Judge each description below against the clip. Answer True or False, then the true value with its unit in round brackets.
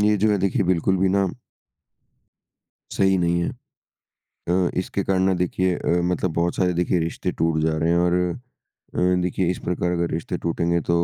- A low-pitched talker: True (90 Hz)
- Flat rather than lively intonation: True (1.5 semitones)